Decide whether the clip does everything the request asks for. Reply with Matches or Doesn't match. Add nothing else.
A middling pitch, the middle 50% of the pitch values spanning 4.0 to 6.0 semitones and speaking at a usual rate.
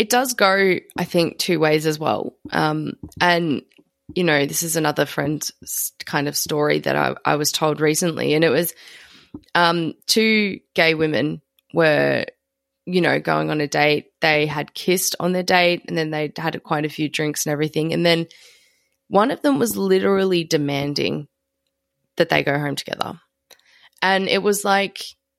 Doesn't match